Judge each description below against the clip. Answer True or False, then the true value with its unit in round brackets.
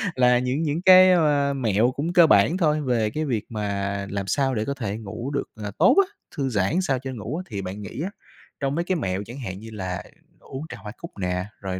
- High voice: False (125 Hz)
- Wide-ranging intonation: True (6.6 semitones)